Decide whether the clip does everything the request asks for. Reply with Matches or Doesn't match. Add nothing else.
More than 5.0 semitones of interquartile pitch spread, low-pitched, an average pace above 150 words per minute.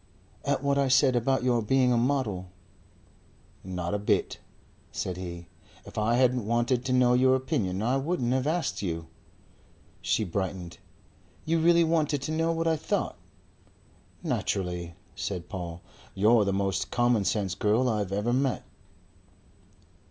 Doesn't match